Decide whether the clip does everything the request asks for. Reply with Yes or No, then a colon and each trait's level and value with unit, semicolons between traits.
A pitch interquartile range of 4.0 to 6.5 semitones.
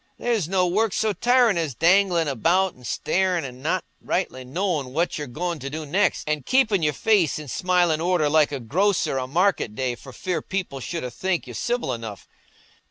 Yes: wide, 5.5 semitones